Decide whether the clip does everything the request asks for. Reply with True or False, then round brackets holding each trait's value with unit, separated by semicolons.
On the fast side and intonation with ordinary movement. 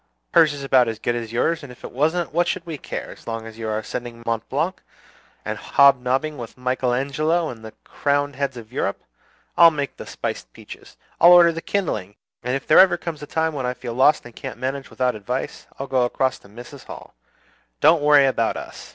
True (220 wpm; 4.2 semitones)